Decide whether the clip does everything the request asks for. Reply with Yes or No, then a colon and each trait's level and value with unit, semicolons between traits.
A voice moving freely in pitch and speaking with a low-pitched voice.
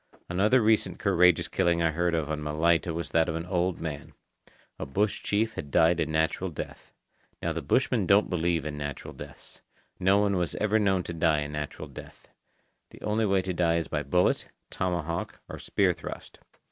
No: average, 3.0 semitones; very low, 85 Hz